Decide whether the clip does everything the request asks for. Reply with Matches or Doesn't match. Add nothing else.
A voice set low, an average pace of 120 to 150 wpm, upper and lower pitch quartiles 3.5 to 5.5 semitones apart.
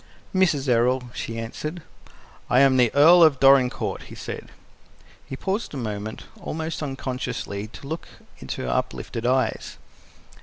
Matches